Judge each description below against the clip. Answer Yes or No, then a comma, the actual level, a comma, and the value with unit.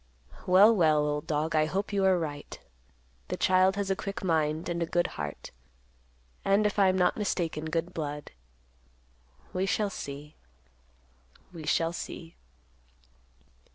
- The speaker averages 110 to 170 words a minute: Yes, average, 145 wpm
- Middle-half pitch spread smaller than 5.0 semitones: Yes, average, 3.8 semitones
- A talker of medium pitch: Yes, medium, 170 Hz